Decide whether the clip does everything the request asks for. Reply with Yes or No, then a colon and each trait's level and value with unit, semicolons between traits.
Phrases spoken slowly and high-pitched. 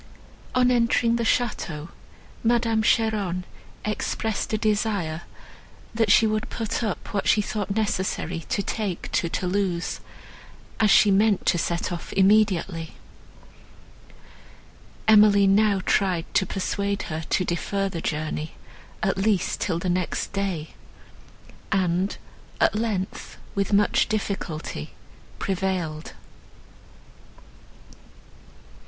Yes: slow, 110 wpm; high, 200 Hz